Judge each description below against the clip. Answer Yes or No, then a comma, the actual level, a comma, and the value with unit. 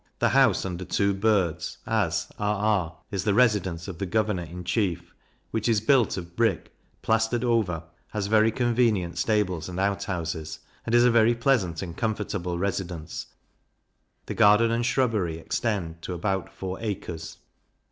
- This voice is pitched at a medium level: No, low, 100 Hz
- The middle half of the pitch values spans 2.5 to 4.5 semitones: Yes, average, 4.2 semitones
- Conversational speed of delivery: Yes, average, 155 wpm